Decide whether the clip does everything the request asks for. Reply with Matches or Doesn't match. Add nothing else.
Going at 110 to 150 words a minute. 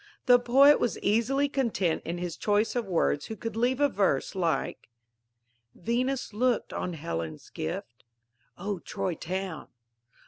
Matches